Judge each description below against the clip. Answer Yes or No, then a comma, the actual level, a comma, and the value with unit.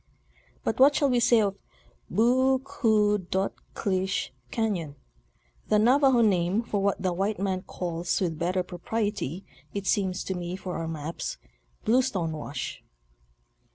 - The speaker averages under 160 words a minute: Yes, average, 150 wpm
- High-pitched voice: Yes, high, 195 Hz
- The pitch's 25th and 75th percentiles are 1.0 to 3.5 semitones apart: No, average, 4.1 semitones